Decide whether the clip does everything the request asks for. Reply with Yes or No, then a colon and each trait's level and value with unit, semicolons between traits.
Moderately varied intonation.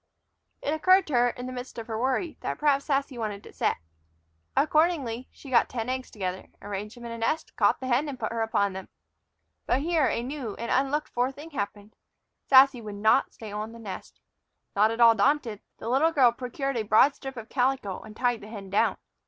Yes: average, 3.8 semitones